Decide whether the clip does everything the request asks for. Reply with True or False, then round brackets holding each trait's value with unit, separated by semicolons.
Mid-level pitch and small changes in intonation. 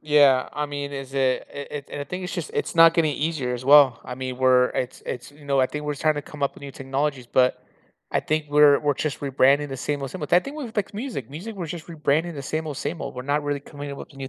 True (145 Hz; 2.3 semitones)